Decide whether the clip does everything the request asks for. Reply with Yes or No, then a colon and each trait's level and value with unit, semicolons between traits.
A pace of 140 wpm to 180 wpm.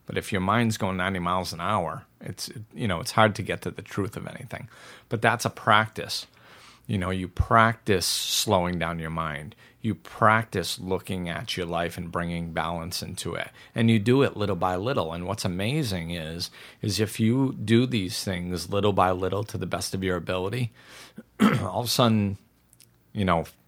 No: average, 195 wpm